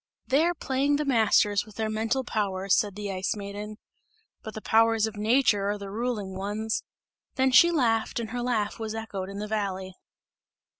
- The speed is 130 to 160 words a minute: No, average, 185 wpm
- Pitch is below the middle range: No, high, 215 Hz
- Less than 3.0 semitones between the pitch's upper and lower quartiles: Yes, narrow, 2.6 semitones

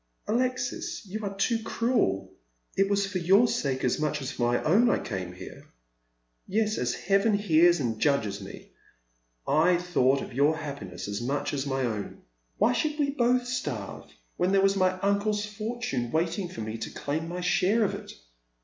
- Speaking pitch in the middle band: Yes, medium, 175 Hz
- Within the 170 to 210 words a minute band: Yes, average, 190 wpm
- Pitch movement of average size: No, wide, 8.0 semitones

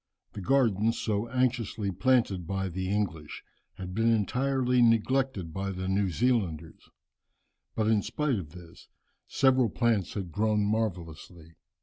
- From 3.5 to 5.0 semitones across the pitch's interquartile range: Yes, average, 4.3 semitones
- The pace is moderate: No, slow, 130 wpm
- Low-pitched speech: Yes, low, 105 Hz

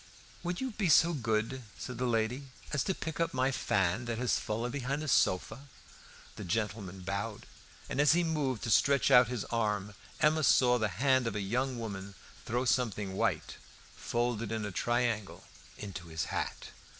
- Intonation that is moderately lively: Yes, average, 4.3 semitones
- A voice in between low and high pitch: No, low, 120 Hz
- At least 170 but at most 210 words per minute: Yes, average, 175 wpm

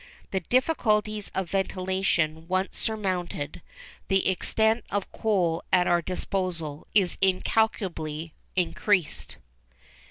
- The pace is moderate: No, slow, 95 wpm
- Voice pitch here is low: No, high, 190 Hz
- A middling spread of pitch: Yes, average, 3.2 semitones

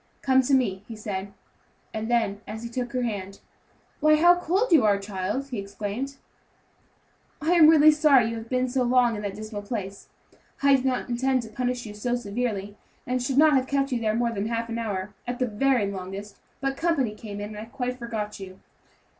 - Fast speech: Yes, fast, 210 wpm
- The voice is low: No, high, 235 Hz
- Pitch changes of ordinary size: Yes, average, 4.1 semitones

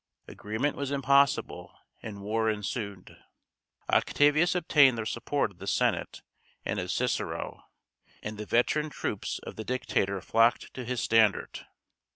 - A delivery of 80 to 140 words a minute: Yes, slow, 135 wpm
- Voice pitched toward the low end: Yes, low, 115 Hz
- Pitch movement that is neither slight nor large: Yes, average, 4.8 semitones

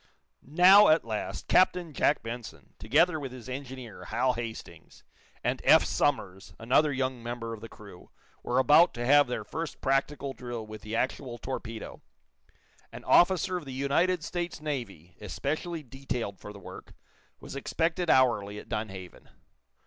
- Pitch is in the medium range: No, low, 130 Hz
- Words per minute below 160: Yes, average, 150 wpm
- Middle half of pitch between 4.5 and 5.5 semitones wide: Yes, average, 5.0 semitones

